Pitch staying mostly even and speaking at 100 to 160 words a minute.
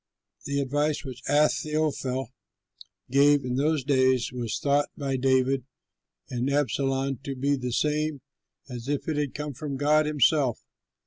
Yes: narrow, 2.1 semitones; average, 140 wpm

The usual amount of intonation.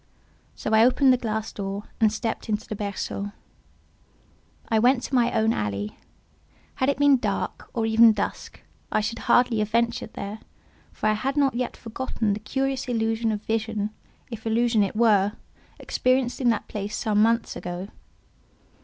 No: narrow, 2.3 semitones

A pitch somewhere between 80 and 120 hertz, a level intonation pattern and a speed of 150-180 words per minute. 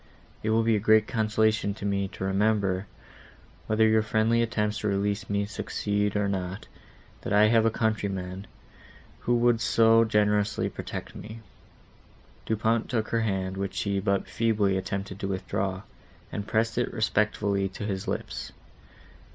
Yes: low, 105 Hz; narrow, 2.0 semitones; average, 155 wpm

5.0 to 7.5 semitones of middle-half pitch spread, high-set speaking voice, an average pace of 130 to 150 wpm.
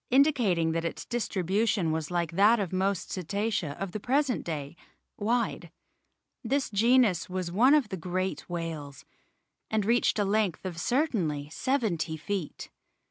Yes: wide, 5.5 semitones; high, 195 Hz; average, 140 wpm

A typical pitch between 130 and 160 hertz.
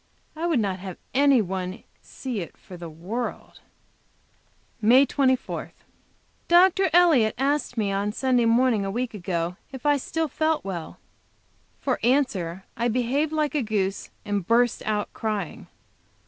No: high, 235 Hz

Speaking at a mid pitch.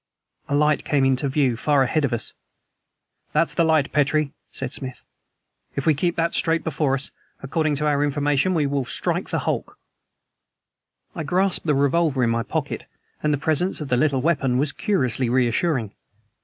Yes: medium, 145 Hz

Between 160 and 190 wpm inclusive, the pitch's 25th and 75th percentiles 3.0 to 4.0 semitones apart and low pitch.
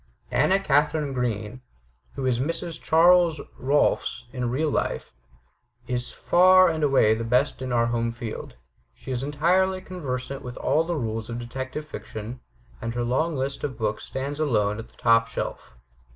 No: average, 165 wpm; average, 4.8 semitones; low, 130 Hz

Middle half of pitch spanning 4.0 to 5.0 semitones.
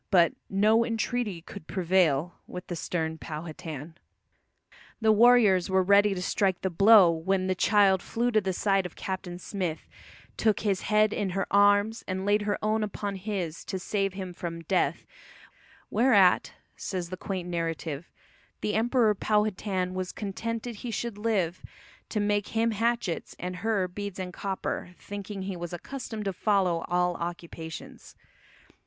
No: average, 3.0 semitones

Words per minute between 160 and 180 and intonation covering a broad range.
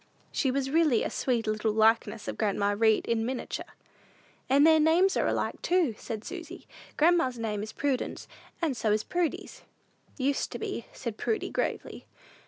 Yes: average, 165 wpm; wide, 6.1 semitones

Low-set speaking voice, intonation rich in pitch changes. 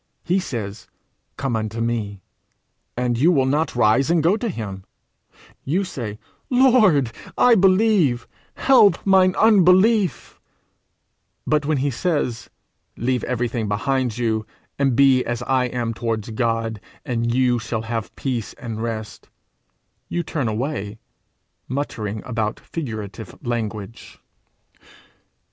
Yes: low, 125 Hz; wide, 5.7 semitones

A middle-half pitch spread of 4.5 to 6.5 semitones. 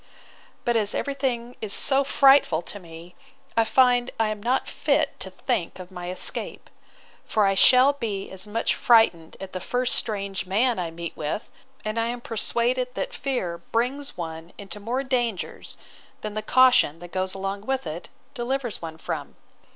Yes: average, 5.2 semitones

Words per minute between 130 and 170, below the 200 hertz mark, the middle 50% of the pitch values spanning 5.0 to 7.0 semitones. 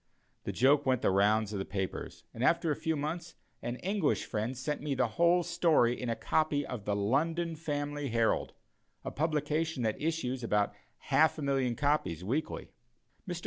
No: average, 185 wpm; medium, 140 Hz; wide, 5.4 semitones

